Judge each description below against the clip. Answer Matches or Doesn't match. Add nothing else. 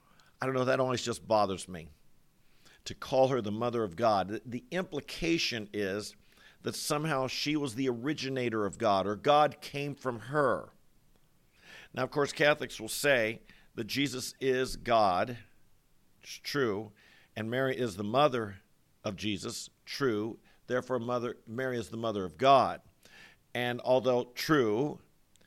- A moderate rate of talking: Matches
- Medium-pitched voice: Doesn't match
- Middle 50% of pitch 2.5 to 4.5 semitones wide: Matches